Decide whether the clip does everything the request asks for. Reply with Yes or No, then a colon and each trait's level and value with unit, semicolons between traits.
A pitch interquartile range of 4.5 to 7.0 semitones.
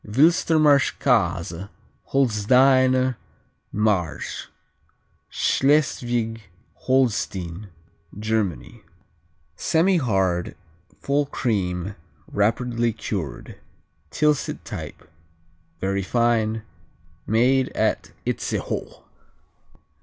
Yes: average, 4.9 semitones